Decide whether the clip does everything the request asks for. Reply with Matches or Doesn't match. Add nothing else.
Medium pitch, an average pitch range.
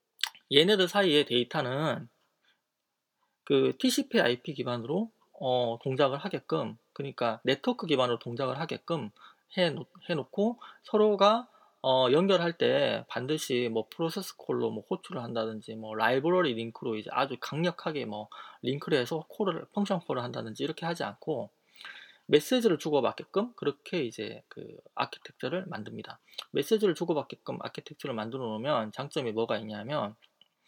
Doesn't match